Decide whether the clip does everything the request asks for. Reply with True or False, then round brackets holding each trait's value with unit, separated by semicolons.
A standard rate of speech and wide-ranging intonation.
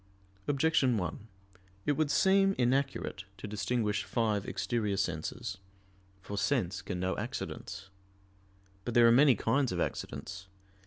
False (125 wpm; 5.7 semitones)